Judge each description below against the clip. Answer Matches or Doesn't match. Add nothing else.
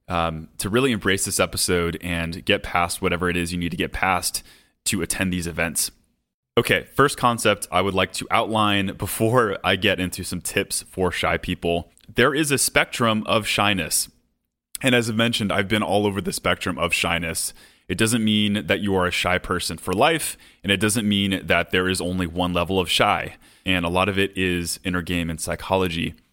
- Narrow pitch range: Doesn't match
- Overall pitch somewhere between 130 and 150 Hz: Doesn't match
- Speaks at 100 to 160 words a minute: Doesn't match